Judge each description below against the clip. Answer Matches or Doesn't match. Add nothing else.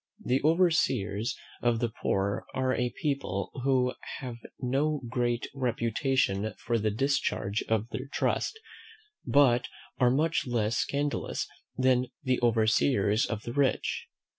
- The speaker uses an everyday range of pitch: Matches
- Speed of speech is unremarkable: Doesn't match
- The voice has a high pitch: Doesn't match